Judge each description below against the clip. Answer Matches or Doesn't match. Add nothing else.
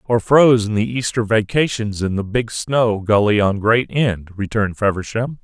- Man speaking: Matches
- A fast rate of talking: Doesn't match